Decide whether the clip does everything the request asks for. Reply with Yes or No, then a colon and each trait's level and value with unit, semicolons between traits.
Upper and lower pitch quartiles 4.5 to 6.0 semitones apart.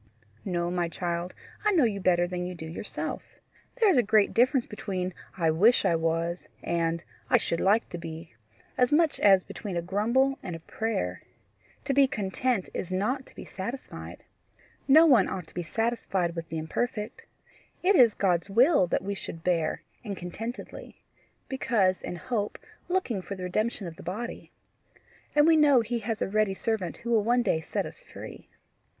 Yes: wide, 5.5 semitones